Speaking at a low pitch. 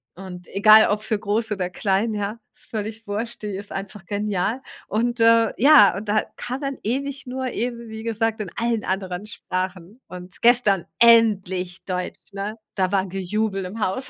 No: high, 210 Hz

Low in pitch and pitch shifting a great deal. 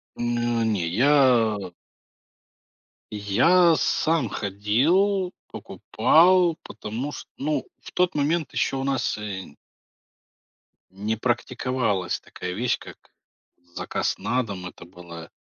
Yes: low, 120 Hz; wide, 6.4 semitones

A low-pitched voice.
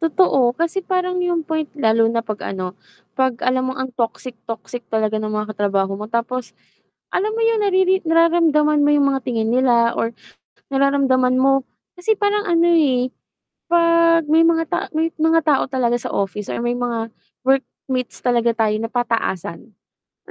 No: very high, 260 Hz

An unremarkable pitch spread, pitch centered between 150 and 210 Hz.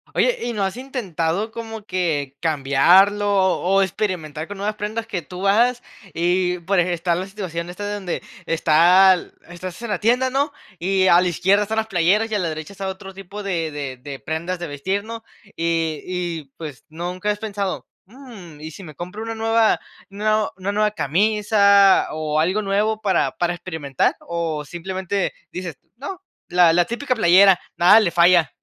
Yes: average, 3.7 semitones; medium, 185 Hz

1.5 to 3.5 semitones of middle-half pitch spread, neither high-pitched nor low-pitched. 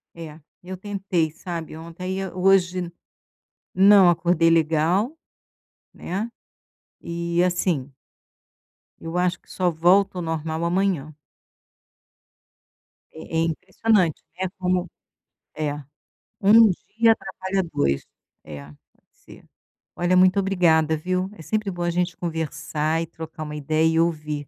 Yes: average, 2.7 semitones; medium, 175 Hz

